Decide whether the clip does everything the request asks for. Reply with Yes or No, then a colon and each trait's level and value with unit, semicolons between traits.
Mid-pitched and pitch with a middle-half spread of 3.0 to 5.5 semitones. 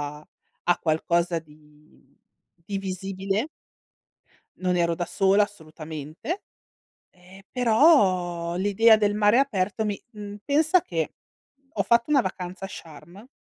No: high, 195 Hz; average, 4.0 semitones